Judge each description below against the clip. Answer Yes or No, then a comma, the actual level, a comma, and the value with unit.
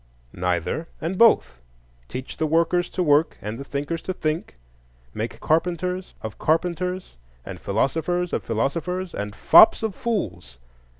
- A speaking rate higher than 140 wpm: No, slow, 135 wpm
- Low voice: No, medium, 165 Hz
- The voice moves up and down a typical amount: No, wide, 7.5 semitones